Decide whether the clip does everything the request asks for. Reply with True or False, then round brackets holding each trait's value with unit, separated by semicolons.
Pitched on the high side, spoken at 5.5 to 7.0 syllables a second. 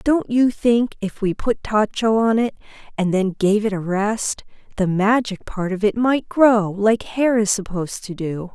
False (210 Hz; 4.2 syllables/s)